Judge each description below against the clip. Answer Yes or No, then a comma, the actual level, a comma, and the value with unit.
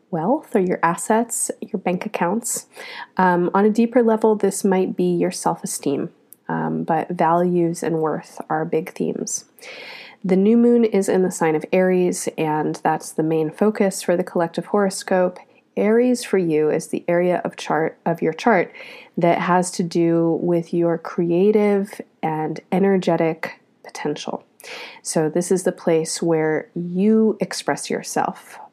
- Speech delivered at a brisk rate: No, average, 150 wpm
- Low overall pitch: No, medium, 180 Hz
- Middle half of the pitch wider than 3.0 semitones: Yes, average, 4.1 semitones